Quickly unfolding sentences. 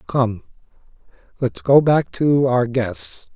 No: average, 145 wpm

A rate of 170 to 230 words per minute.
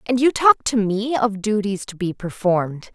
Yes: fast, 205 wpm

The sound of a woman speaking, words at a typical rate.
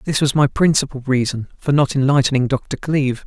No: male; average, 185 wpm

